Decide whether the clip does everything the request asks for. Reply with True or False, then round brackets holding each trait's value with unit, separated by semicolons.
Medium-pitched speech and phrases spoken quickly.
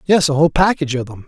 True (155 Hz; 280 wpm)